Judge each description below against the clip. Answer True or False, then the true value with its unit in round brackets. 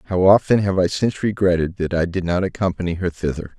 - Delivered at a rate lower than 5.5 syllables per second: False (6.2 syllables/s)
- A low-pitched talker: True (90 Hz)